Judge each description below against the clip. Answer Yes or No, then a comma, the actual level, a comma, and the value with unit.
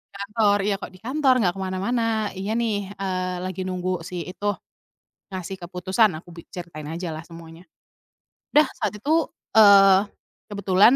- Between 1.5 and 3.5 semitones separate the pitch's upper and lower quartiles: Yes, narrow, 2.5 semitones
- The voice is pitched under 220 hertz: Yes, high, 190 Hz